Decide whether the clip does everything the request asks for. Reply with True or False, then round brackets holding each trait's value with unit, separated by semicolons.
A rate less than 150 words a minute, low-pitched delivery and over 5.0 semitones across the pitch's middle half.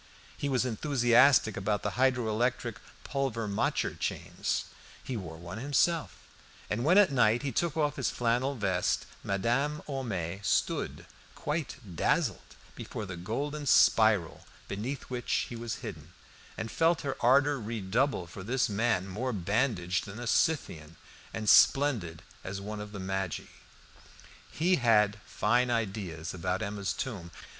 True (140 wpm; 115 Hz; 5.4 semitones)